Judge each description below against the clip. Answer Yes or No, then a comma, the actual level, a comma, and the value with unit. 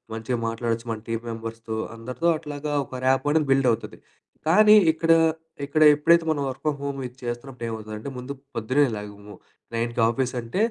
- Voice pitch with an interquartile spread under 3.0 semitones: No, average, 3.9 semitones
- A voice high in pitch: No, low, 125 Hz